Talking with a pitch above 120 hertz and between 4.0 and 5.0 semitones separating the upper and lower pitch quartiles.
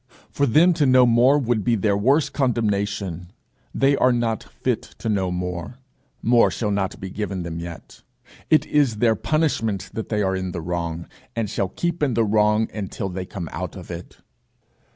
No: low, 105 Hz; average, 4.7 semitones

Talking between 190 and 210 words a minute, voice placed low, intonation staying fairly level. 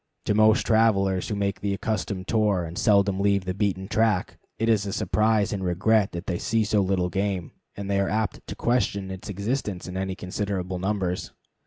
Yes: average, 195 wpm; low, 100 Hz; narrow, 2.2 semitones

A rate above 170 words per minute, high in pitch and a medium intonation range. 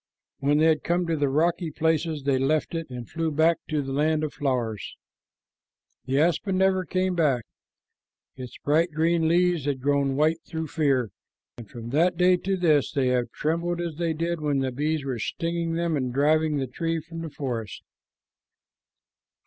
No: average, 180 wpm; medium, 155 Hz; average, 3.4 semitones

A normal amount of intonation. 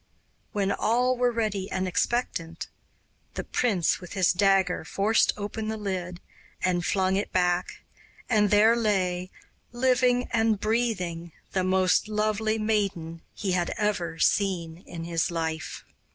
Yes: average, 3.5 semitones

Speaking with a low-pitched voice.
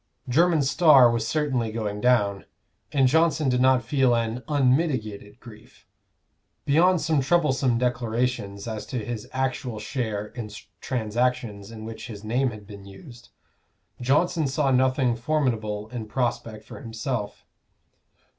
Yes: low, 125 Hz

